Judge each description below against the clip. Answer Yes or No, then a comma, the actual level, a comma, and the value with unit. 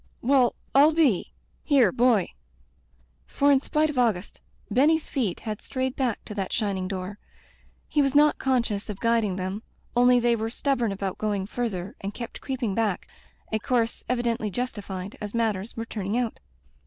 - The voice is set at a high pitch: Yes, high, 230 Hz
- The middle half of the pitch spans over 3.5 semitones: Yes, average, 4.0 semitones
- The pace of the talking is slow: No, average, 165 wpm